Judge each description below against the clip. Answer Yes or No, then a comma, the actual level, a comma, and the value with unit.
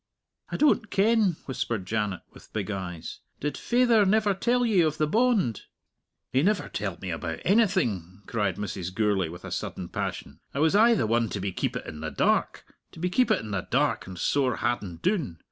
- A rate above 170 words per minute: Yes, average, 195 wpm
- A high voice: No, low, 120 Hz